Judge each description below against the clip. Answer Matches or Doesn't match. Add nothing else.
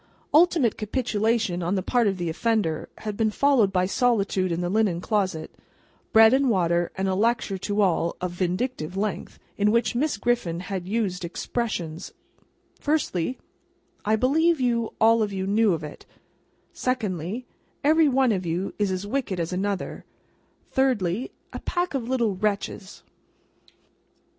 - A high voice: Matches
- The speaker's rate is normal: Matches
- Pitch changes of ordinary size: Matches